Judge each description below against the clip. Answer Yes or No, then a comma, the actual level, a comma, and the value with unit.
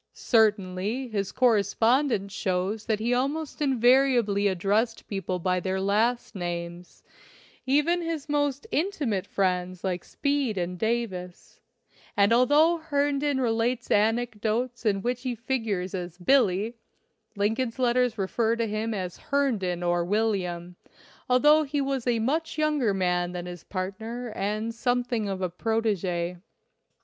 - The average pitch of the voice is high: Yes, high, 225 Hz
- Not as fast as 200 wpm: Yes, slow, 135 wpm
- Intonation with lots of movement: No, average, 5.0 semitones